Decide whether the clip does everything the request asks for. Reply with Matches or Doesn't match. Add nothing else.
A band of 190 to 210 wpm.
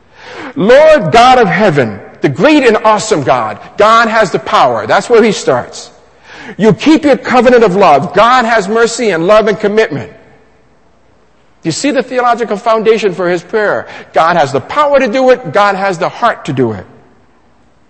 Doesn't match